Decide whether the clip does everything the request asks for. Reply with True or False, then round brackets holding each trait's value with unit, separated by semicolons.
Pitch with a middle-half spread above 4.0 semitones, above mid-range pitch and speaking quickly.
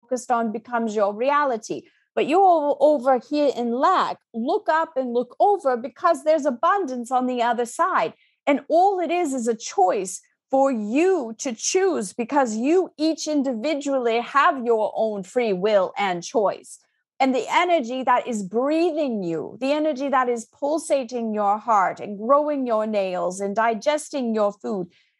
False (5.2 semitones; 260 Hz; 160 wpm)